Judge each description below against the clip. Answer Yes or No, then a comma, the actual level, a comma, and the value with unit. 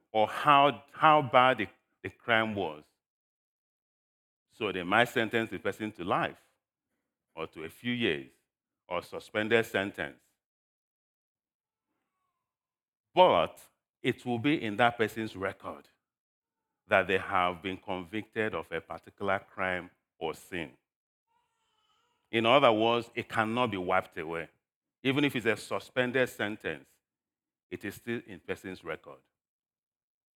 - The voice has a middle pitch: No, low, 110 Hz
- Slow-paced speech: Yes, slow, 125 wpm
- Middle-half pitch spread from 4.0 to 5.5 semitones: Yes, average, 4.9 semitones